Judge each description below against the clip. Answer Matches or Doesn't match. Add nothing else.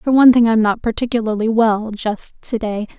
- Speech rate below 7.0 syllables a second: Matches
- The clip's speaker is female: Matches